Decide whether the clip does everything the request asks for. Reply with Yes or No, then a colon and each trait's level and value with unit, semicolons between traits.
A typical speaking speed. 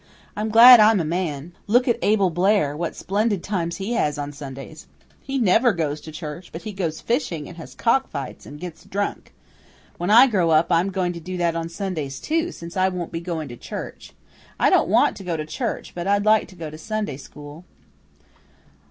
No: fast, 210 wpm